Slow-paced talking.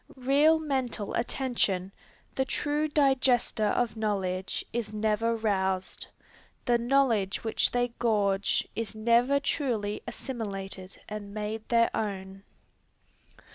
Yes: slow, 105 wpm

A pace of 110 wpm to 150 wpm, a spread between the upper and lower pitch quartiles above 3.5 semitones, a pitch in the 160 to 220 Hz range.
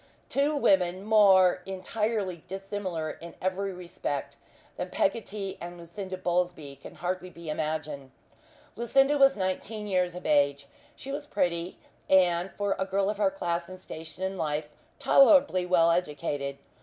No: average, 145 wpm; average, 2.9 semitones; medium, 185 Hz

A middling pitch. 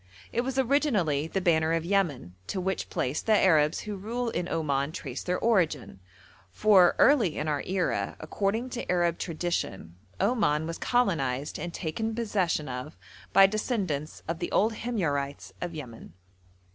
Yes: medium, 175 Hz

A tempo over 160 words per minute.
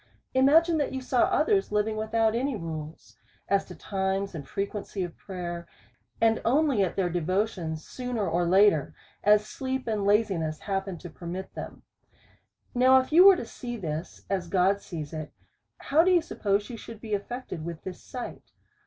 Yes: average, 170 wpm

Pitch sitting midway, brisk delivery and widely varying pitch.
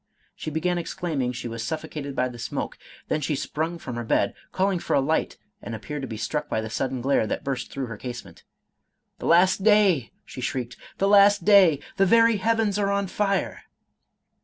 Yes: medium, 155 Hz; fast, 210 wpm; wide, 7.6 semitones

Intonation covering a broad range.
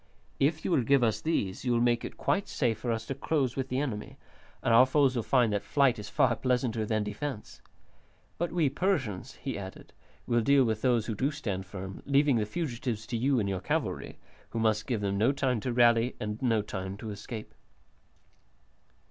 No: average, 4.0 semitones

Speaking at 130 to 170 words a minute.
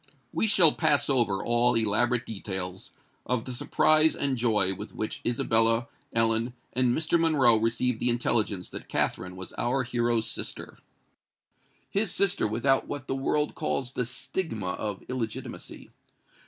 Yes: average, 140 wpm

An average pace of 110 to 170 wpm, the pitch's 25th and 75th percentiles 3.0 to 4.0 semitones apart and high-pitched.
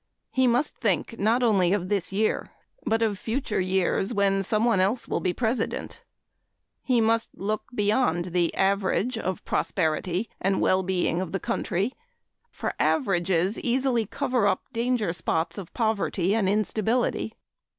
Yes: average, 150 wpm; average, 3.6 semitones; high, 205 Hz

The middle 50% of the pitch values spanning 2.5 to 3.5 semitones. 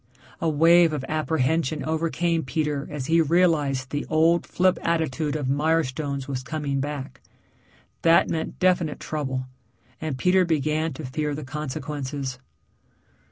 Yes: average, 2.8 semitones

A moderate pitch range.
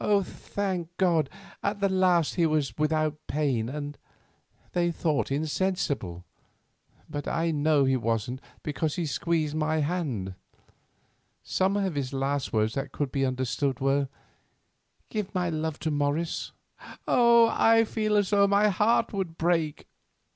Yes: average, 4.9 semitones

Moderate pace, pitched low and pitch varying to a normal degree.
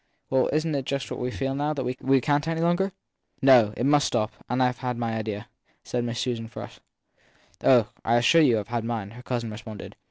No: fast, 215 wpm; low, 125 Hz; average, 3.0 semitones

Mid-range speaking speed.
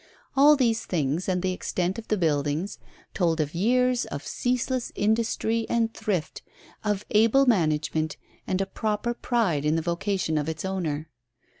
Yes: average, 155 wpm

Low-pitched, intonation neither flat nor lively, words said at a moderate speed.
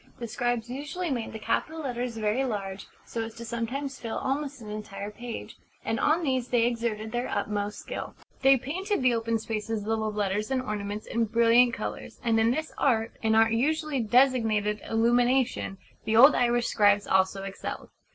No: high, 230 Hz; average, 3.1 semitones; average, 180 wpm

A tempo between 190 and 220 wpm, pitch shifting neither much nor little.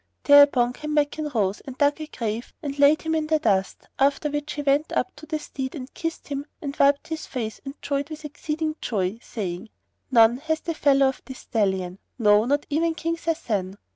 Yes: average, 200 wpm; average, 4.8 semitones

